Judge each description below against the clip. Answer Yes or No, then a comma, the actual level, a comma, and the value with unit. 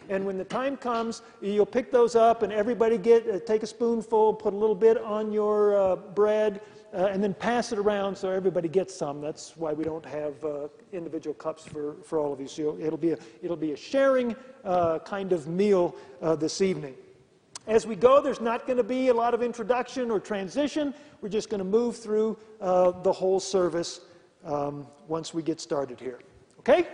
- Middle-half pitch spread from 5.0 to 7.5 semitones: Yes, wide, 5.6 semitones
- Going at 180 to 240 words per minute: Yes, fast, 205 wpm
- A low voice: No, high, 200 Hz